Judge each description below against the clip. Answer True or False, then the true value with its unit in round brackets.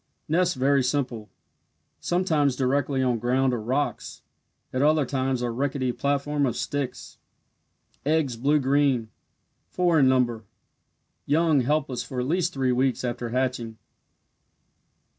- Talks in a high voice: False (135 Hz)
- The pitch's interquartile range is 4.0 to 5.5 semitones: False (2.7 semitones)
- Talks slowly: True (125 wpm)